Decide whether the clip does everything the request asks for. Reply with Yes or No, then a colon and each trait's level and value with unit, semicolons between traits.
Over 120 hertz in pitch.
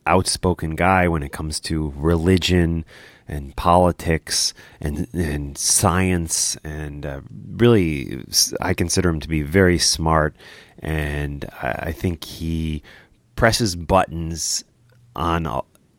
No: very low, 85 Hz